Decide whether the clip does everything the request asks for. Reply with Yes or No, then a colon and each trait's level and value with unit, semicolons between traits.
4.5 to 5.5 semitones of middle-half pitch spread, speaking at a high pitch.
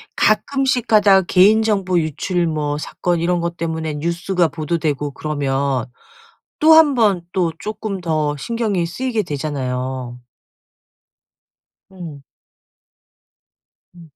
No: average, 5.2 semitones; medium, 170 Hz